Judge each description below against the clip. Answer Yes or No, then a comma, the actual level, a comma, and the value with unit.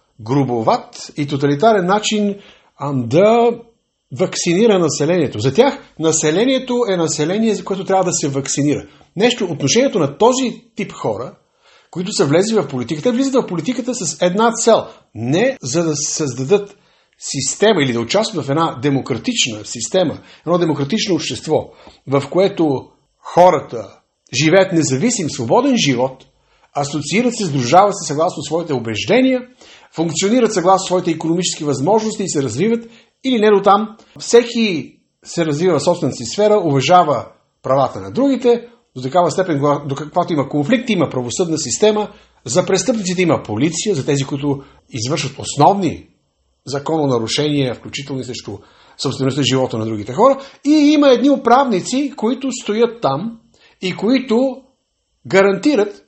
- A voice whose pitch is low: No, medium, 180 Hz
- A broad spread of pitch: Yes, wide, 7.8 semitones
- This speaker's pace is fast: No, average, 135 wpm